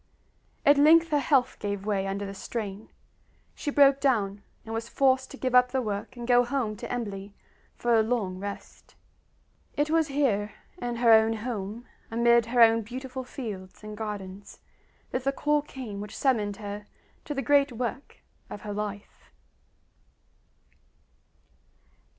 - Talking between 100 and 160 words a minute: Yes, average, 155 wpm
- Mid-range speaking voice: No, high, 230 Hz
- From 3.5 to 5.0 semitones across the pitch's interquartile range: Yes, average, 4.2 semitones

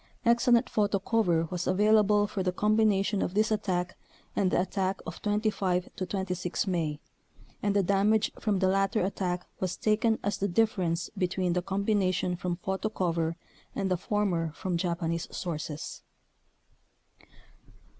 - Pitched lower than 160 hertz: No, high, 190 Hz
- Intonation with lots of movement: No, average, 2.7 semitones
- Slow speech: No, average, 145 wpm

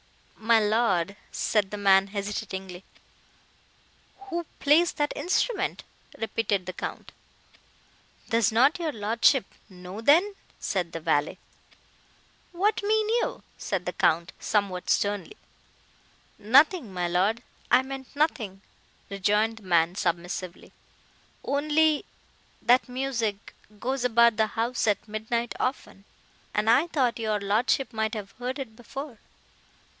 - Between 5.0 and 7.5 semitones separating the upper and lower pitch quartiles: Yes, average, 5.3 semitones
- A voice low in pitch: No, high, 225 Hz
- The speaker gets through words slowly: Yes, slow, 115 wpm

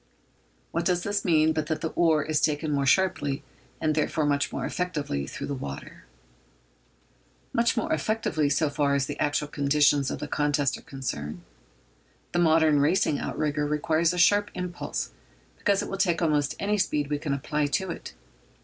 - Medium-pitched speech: Yes, medium, 150 Hz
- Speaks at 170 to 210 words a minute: Yes, average, 175 wpm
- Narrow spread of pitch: No, average, 3.2 semitones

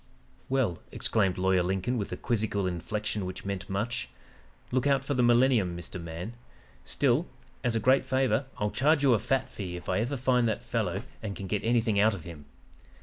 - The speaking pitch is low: Yes, low, 110 Hz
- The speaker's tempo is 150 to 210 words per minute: Yes, average, 195 wpm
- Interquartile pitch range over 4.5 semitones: Yes, average, 5.0 semitones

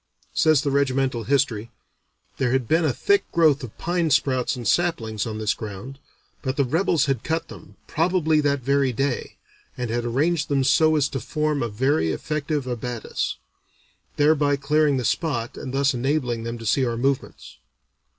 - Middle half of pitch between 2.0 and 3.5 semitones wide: No, average, 4.0 semitones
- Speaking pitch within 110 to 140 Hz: Yes, low, 135 Hz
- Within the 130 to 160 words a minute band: No, average, 170 wpm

